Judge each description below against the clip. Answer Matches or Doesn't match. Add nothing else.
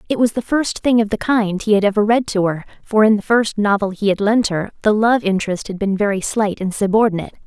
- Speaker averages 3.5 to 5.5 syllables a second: Doesn't match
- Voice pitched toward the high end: Matches